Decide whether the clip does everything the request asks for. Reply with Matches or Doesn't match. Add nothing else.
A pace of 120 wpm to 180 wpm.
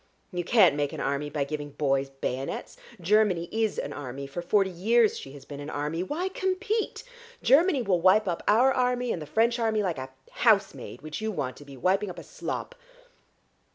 Doesn't match